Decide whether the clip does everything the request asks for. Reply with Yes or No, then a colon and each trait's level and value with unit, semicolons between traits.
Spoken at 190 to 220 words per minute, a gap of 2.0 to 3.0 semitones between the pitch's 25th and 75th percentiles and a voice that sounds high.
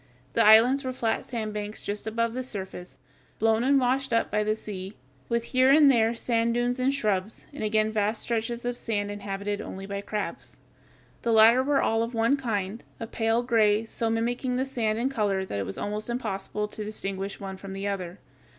Yes: average, 200 wpm; average, 2.7 semitones; high, 220 Hz